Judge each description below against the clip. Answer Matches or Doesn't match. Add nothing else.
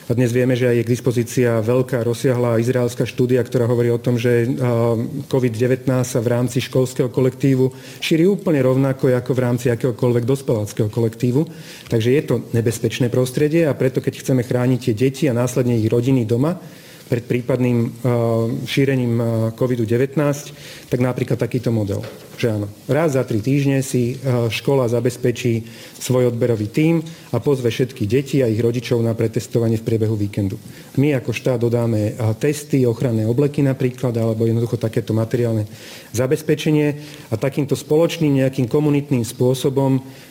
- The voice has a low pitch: Matches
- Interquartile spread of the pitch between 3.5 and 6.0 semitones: Doesn't match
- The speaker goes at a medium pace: Matches